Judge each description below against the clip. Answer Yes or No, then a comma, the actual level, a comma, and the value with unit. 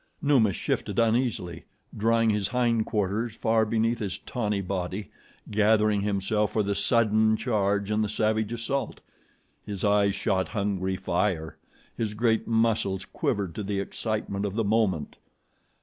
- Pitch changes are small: Yes, narrow, 2.2 semitones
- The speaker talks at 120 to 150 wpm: Yes, average, 140 wpm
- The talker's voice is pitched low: Yes, low, 105 Hz